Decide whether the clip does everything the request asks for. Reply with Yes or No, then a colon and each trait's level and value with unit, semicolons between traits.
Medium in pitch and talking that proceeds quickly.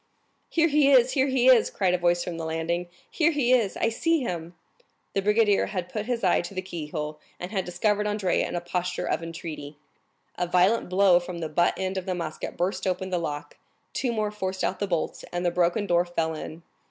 Yes: medium, 180 Hz; fast, 220 wpm